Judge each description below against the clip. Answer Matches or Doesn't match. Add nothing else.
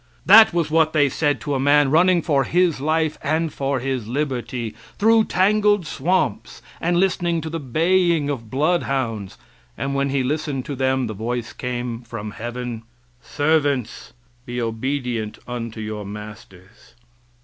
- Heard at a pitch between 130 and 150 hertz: Matches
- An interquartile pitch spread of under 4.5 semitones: Doesn't match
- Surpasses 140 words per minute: Matches